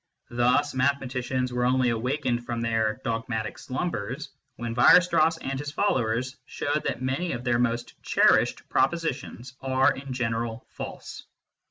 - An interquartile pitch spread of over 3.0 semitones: No, narrow, 2.6 semitones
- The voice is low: Yes, low, 125 Hz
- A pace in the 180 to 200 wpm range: No, average, 150 wpm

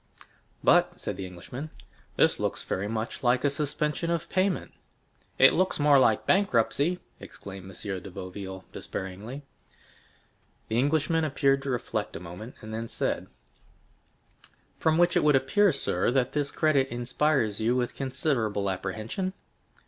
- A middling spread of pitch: No, wide, 6.2 semitones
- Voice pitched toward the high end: No, low, 130 Hz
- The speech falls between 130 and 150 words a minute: Yes, average, 140 wpm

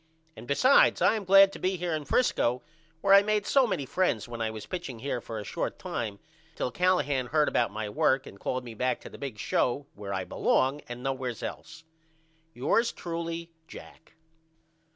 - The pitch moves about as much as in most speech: No, wide, 7.0 semitones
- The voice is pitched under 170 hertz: Yes, medium, 140 Hz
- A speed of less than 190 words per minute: No, average, 195 wpm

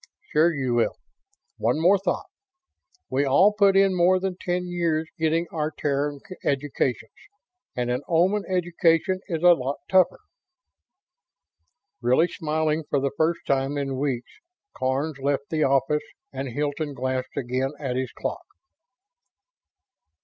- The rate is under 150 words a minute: Yes, slow, 135 wpm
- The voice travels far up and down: No, average, 4.3 semitones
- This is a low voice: No, medium, 150 Hz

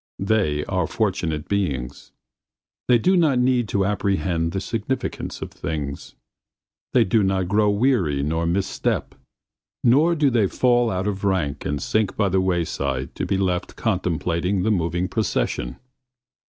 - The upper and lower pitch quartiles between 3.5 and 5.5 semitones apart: Yes, average, 4.8 semitones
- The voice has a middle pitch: No, very low, 95 Hz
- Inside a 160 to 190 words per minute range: No, average, 150 wpm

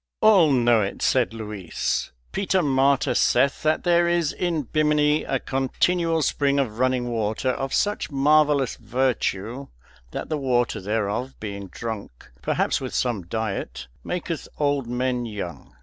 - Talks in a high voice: No, low, 130 Hz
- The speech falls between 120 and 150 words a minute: Yes, average, 140 wpm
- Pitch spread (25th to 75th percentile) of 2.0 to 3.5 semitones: No, average, 5.1 semitones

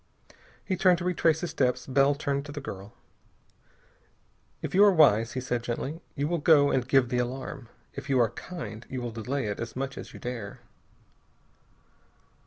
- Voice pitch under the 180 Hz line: Yes, low, 135 Hz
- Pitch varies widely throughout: No, average, 4.0 semitones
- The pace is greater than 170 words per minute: Yes, average, 185 wpm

